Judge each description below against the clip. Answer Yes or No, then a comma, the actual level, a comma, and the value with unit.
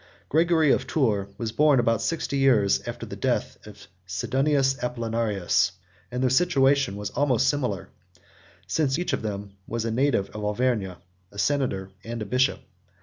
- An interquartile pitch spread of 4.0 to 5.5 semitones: Yes, average, 4.8 semitones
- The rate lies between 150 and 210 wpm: Yes, average, 160 wpm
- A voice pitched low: Yes, low, 125 Hz